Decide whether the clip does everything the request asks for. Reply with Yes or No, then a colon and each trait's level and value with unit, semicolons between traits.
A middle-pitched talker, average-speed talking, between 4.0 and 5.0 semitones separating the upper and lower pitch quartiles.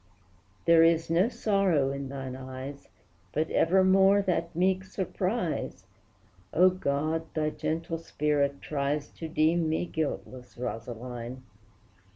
No: medium, 160 Hz; slow, 115 wpm; average, 4.3 semitones